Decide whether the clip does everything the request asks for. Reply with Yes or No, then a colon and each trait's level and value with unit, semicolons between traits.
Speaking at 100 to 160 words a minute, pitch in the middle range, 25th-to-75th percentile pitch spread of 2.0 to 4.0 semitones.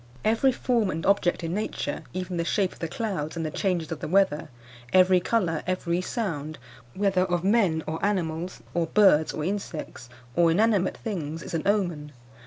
No: average, 180 wpm; medium, 180 Hz; average, 3.5 semitones